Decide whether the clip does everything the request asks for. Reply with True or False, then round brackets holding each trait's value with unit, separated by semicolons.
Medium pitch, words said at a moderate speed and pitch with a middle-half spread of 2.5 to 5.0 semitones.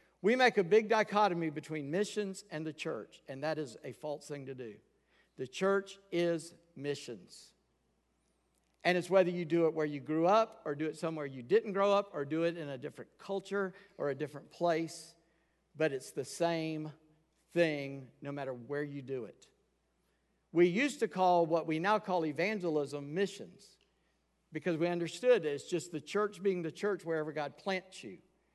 True (165 Hz; 180 wpm; 4.3 semitones)